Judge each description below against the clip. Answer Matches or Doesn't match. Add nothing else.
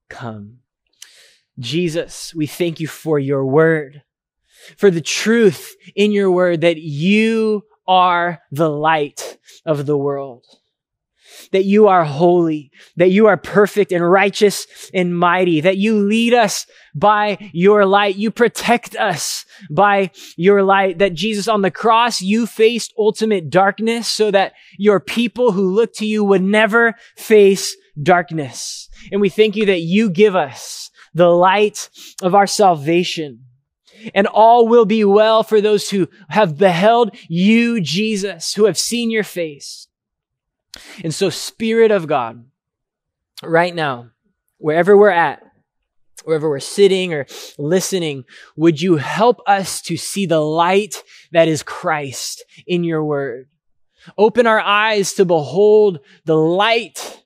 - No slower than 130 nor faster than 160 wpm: Matches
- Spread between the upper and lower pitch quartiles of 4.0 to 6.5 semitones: Matches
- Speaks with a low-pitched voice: Doesn't match